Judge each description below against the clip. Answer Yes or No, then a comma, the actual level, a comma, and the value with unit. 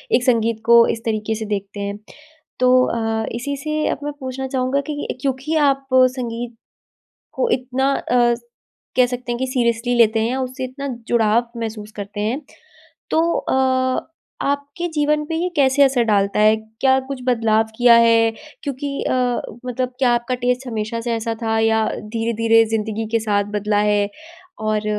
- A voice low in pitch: No, high, 240 Hz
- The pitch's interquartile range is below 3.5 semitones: Yes, average, 2.9 semitones